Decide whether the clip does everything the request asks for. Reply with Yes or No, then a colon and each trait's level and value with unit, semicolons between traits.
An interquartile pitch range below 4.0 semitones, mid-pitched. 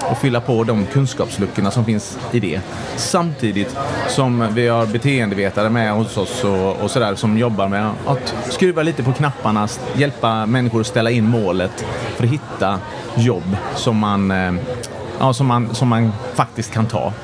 No: average, 3.1 semitones; low, 115 Hz